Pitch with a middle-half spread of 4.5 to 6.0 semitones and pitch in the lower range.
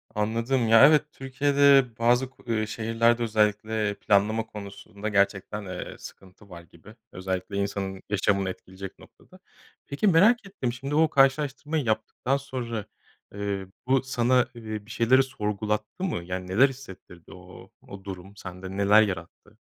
Yes: average, 4.8 semitones; low, 110 Hz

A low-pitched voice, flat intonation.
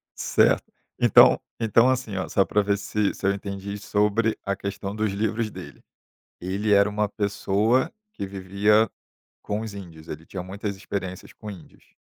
Yes: low, 100 Hz; narrow, 1.5 semitones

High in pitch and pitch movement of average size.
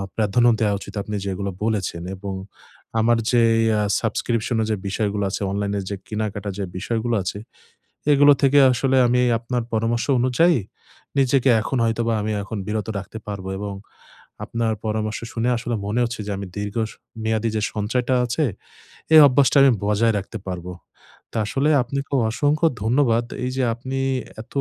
No: low, 115 Hz; average, 3.0 semitones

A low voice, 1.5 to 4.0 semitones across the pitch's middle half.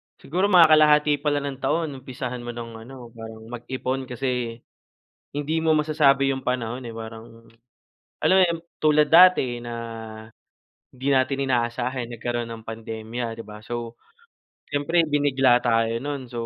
Yes: low, 130 Hz; average, 3.7 semitones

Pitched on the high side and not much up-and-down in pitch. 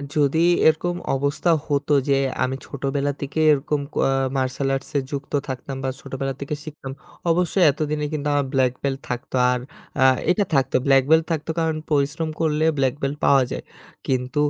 No: medium, 140 Hz; narrow, 2.2 semitones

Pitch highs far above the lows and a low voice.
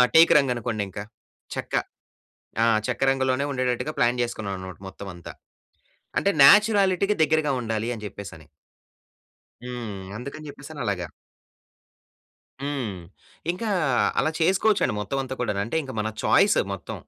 Yes: wide, 6.3 semitones; low, 125 Hz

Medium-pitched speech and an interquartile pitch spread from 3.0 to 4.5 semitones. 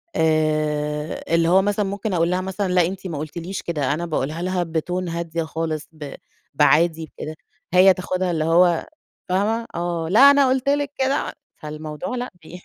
Yes: medium, 170 Hz; average, 3.3 semitones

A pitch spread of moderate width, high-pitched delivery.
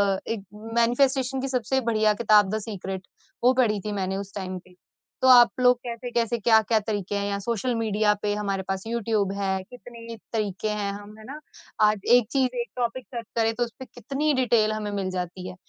Yes: average, 3.2 semitones; high, 220 Hz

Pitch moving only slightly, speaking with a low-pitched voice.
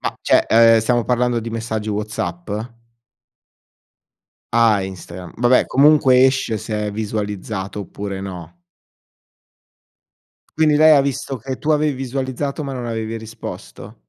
No: average, 4.0 semitones; low, 115 Hz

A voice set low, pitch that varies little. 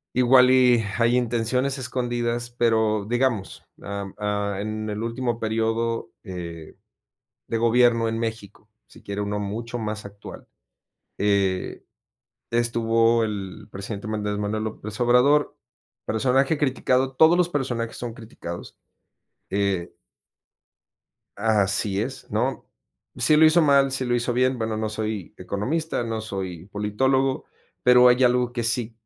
No: low, 115 Hz; average, 3.2 semitones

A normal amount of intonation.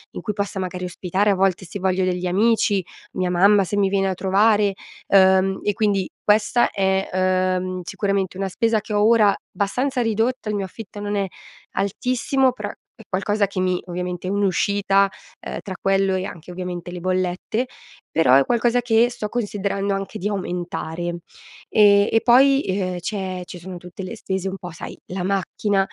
No: narrow, 2.1 semitones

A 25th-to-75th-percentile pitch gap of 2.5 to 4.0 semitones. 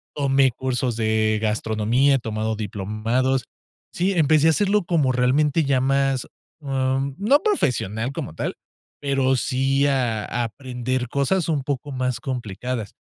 Yes: average, 3.3 semitones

